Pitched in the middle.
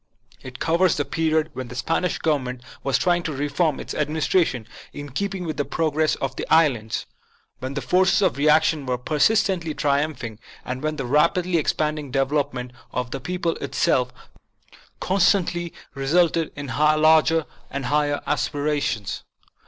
Yes: medium, 150 Hz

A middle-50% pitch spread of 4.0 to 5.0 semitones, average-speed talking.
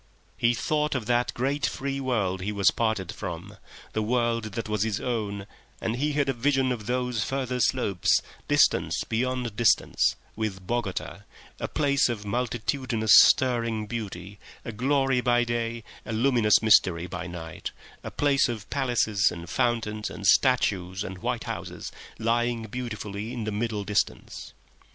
No: average, 3.3 semitones; average, 155 wpm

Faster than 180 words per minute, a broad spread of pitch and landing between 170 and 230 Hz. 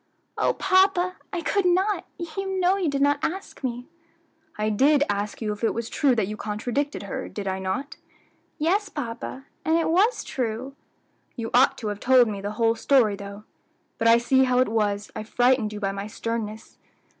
No: average, 190 wpm; wide, 6.4 semitones; high, 245 Hz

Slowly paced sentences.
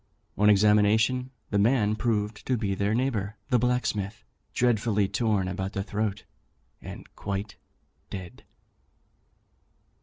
Yes: slow, 115 wpm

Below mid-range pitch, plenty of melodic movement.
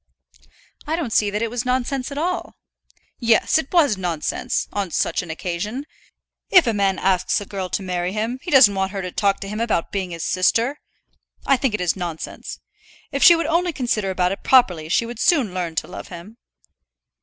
No: high, 210 Hz; wide, 6.0 semitones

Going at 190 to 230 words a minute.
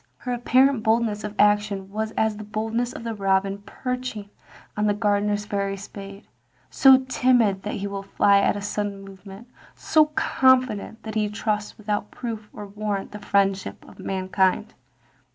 No: average, 165 wpm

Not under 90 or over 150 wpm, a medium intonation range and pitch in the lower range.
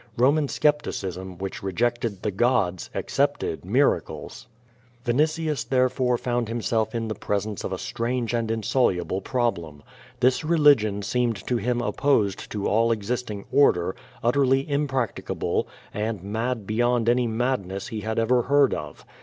Yes: slow, 135 wpm; average, 3.6 semitones; low, 115 Hz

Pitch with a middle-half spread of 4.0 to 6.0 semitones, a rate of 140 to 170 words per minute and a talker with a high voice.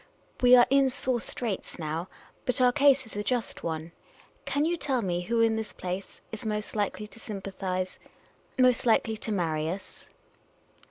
No: average, 5.1 semitones; average, 180 wpm; high, 220 Hz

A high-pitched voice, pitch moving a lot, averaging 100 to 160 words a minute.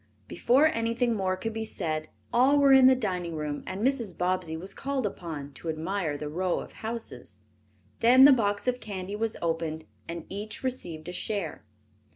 No: high, 195 Hz; wide, 6.1 semitones; average, 180 wpm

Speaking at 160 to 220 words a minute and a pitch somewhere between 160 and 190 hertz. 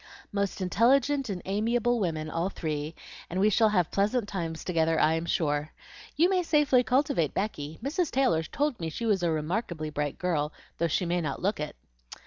Yes: average, 185 wpm; medium, 185 Hz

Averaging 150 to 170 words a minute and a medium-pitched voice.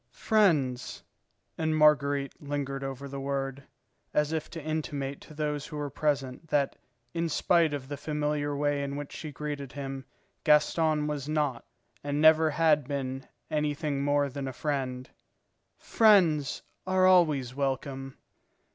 No: average, 140 wpm; medium, 145 Hz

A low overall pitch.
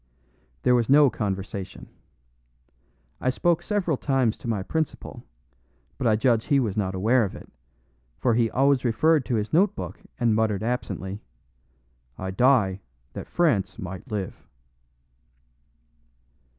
Yes: low, 115 Hz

